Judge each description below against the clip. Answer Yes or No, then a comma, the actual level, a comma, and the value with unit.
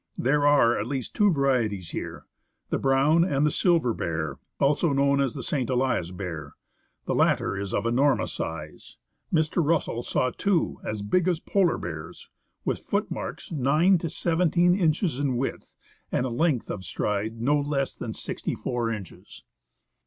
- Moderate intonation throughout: No, wide, 5.7 semitones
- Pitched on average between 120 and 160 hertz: Yes, low, 135 Hz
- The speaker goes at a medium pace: Yes, average, 165 wpm